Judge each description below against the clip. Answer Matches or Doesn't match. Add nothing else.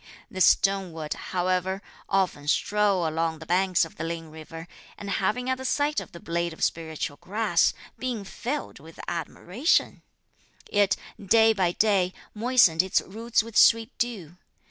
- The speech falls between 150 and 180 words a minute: Matches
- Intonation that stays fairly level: Doesn't match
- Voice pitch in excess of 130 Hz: Matches